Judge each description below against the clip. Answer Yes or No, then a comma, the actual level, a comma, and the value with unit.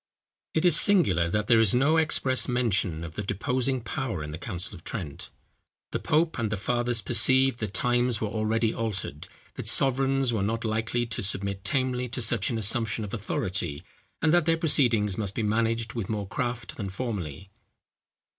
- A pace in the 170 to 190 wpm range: Yes, average, 180 wpm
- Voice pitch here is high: No, low, 115 Hz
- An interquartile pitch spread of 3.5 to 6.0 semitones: Yes, average, 4.0 semitones